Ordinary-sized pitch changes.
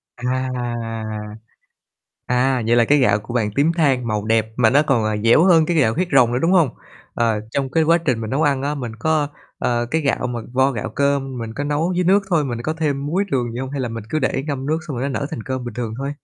Yes: average, 3.9 semitones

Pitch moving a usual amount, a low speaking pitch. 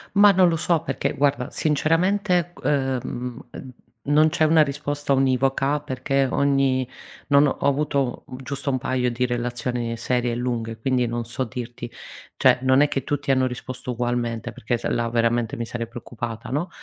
Yes: average, 3.0 semitones; low, 130 Hz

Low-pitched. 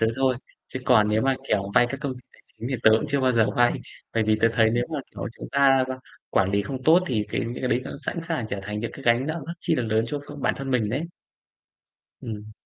Yes: low, 120 Hz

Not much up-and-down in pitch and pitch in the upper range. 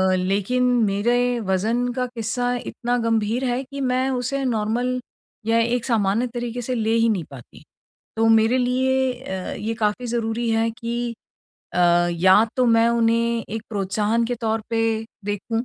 Yes: narrow, 2.1 semitones; high, 230 Hz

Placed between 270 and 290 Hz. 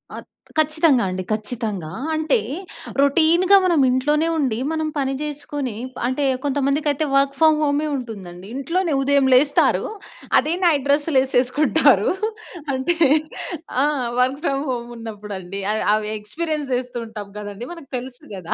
Yes: very high, 275 Hz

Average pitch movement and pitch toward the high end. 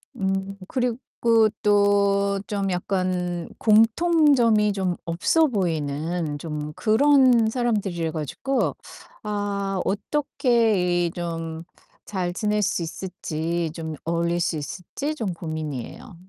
Yes: average, 4.6 semitones; high, 195 Hz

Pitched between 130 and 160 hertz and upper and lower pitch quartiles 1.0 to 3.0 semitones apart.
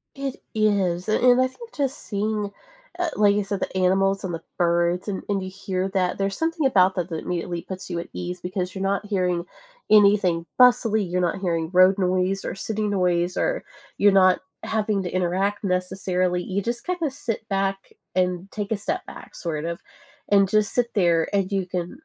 No: high, 195 Hz; narrow, 2.5 semitones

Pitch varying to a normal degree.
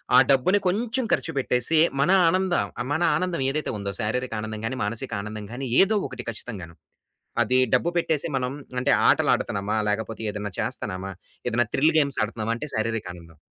No: wide, 6.3 semitones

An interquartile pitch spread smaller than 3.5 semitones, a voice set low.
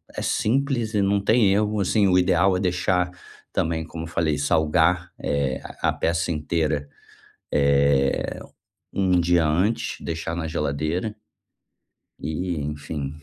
No: average, 3.9 semitones; very low, 85 Hz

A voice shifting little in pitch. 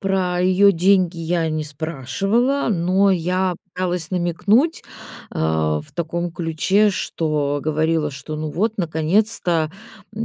No: average, 3.6 semitones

